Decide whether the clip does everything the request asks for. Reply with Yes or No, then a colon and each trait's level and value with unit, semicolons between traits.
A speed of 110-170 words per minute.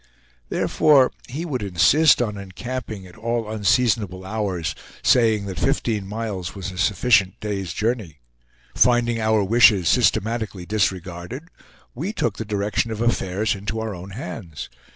Yes: slow, 135 wpm